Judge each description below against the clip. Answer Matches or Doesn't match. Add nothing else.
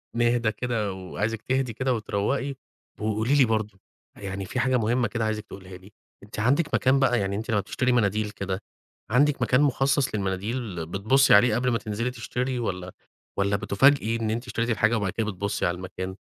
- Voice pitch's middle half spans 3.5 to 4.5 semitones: Matches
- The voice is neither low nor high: Doesn't match